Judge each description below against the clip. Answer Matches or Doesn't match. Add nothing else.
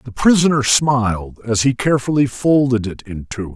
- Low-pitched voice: Matches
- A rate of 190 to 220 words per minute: Doesn't match